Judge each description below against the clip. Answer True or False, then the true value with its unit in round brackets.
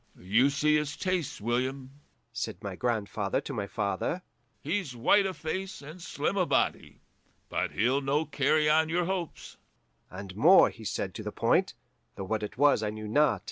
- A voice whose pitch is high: False (140 Hz)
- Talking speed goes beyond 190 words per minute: False (180 wpm)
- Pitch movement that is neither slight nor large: False (6.5 semitones)